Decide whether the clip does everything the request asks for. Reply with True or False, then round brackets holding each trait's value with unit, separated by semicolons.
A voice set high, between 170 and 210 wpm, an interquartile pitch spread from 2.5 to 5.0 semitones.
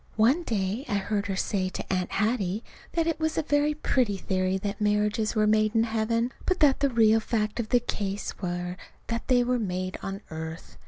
True (215 Hz; 205 wpm; 3.8 semitones)